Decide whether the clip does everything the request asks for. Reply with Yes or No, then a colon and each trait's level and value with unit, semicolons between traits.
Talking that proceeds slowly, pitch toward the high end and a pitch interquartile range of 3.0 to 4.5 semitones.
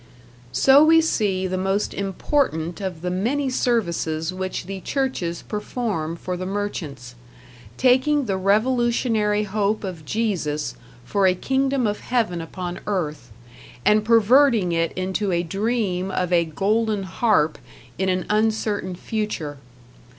Yes: slow, 130 wpm; high, 200 Hz; average, 4.1 semitones